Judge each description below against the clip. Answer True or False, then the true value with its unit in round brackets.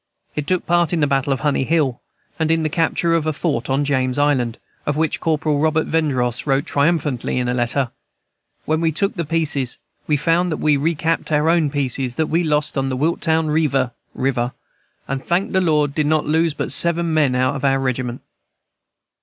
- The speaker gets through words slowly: False (200 wpm)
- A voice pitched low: False (150 Hz)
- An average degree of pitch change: True (3.2 semitones)